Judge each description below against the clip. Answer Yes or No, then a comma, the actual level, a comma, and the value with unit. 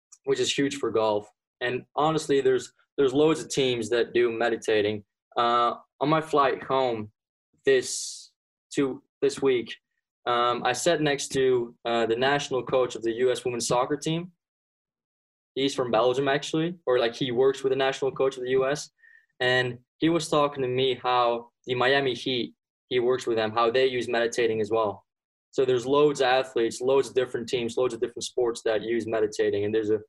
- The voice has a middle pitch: No, low, 130 Hz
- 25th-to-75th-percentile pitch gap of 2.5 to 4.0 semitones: No, average, 5.1 semitones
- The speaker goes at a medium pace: Yes, average, 185 wpm